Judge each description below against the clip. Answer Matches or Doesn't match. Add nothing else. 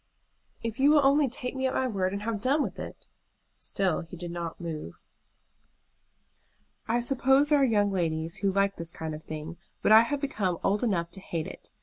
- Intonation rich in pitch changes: Matches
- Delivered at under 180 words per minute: Doesn't match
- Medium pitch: Doesn't match